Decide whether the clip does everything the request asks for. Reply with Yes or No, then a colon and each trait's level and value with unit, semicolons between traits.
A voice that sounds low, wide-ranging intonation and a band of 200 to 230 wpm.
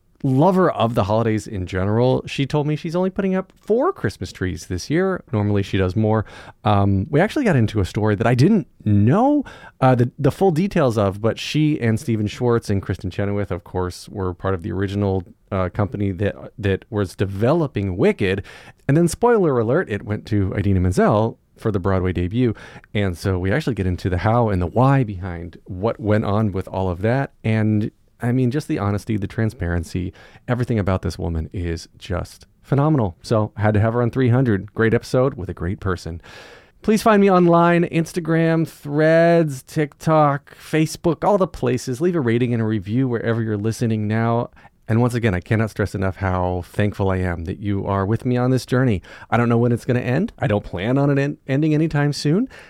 Yes: low, 110 Hz; wide, 5.9 semitones; fast, 205 wpm